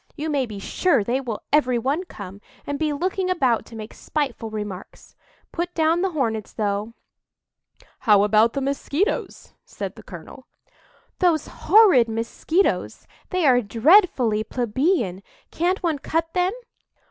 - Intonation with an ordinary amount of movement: No, wide, 7.3 semitones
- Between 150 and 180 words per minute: No, slow, 135 wpm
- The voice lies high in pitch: Yes, very high, 270 Hz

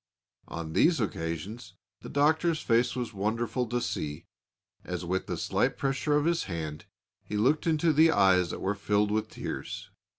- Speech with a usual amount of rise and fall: No, wide, 7.7 semitones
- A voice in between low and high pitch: No, low, 110 Hz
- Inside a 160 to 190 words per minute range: Yes, average, 165 wpm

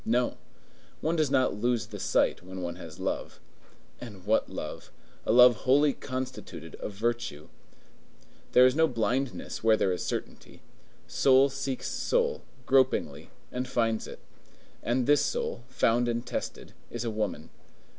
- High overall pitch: No, low, 120 Hz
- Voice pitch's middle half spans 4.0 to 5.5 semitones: No, average, 3.0 semitones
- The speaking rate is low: No, average, 145 wpm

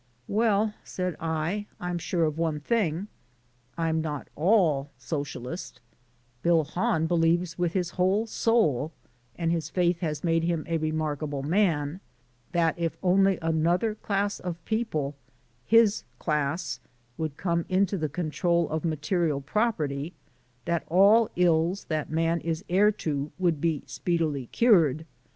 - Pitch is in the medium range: Yes, medium, 165 Hz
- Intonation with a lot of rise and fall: No, average, 3.0 semitones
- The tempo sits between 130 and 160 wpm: Yes, slow, 135 wpm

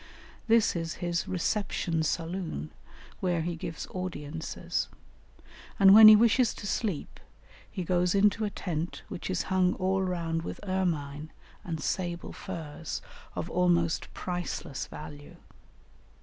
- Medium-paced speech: No, slow, 125 wpm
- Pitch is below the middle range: No, medium, 175 Hz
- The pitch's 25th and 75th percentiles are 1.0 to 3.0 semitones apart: Yes, narrow, 2.6 semitones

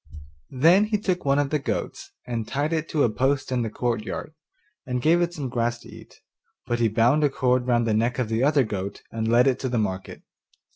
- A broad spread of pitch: No, average, 3.9 semitones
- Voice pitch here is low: Yes, low, 125 Hz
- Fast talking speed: Yes, fast, 230 wpm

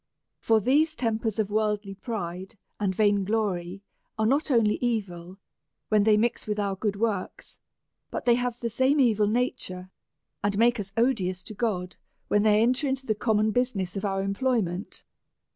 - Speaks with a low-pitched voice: No, high, 215 Hz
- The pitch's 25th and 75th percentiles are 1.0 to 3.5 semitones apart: Yes, average, 3.1 semitones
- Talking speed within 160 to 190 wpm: Yes, average, 170 wpm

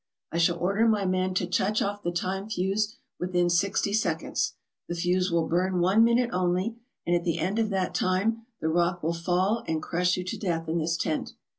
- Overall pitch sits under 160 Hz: No, medium, 180 Hz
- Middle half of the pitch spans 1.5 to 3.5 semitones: Yes, narrow, 2.5 semitones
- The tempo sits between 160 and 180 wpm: No, fast, 205 wpm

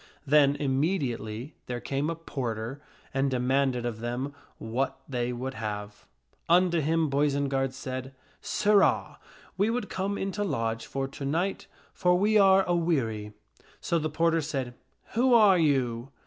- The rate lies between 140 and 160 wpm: Yes, average, 155 wpm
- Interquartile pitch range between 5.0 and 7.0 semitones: Yes, wide, 5.5 semitones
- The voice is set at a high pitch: No, medium, 140 Hz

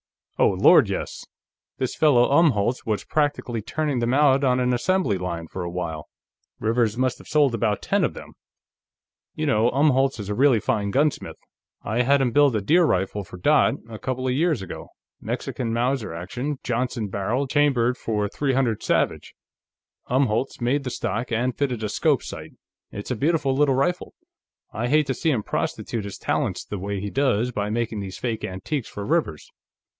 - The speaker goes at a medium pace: Yes, average, 180 wpm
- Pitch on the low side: Yes, low, 125 Hz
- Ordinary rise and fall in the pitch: Yes, average, 4.7 semitones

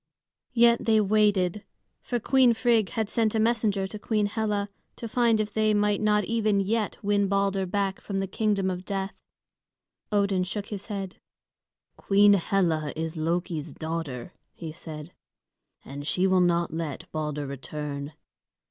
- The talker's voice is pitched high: Yes, high, 195 Hz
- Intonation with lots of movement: No, average, 3.8 semitones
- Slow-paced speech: No, average, 150 wpm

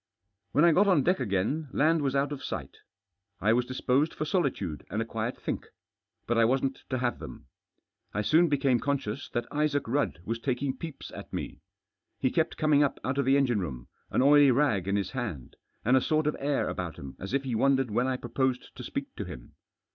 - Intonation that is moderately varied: Yes, average, 4.1 semitones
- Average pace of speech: No, fast, 210 wpm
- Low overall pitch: Yes, low, 130 Hz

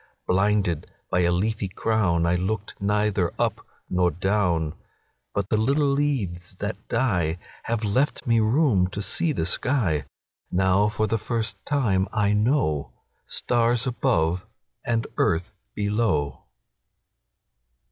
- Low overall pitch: Yes, low, 100 Hz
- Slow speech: Yes, slow, 105 wpm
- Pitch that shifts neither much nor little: Yes, average, 4.3 semitones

